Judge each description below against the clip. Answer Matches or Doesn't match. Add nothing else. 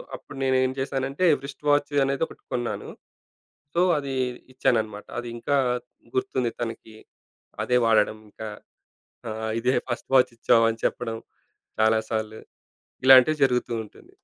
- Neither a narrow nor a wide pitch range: Matches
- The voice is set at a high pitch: Doesn't match